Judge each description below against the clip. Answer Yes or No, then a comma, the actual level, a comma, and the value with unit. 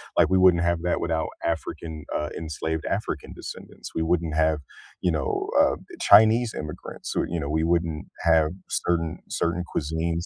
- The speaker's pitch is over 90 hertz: No, very low, 80 Hz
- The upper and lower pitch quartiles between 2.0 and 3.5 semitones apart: No, narrow, 1.5 semitones